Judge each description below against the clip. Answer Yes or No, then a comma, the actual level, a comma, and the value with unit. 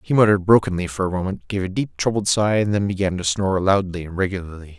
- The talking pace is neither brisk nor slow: No, fast, 240 wpm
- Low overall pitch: Yes, very low, 95 Hz